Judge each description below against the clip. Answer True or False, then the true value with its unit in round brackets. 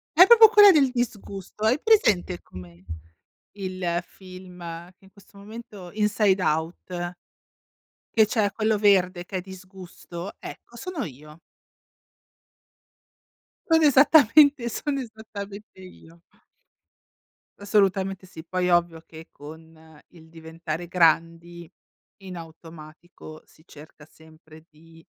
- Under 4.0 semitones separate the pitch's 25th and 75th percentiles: False (4.5 semitones)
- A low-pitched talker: False (185 Hz)